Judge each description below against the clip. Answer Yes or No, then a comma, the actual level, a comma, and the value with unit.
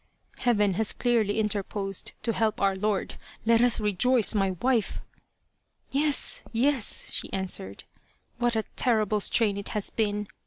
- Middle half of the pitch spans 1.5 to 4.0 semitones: Yes, average, 2.8 semitones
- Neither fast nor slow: Yes, average, 155 wpm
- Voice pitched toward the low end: No, high, 215 Hz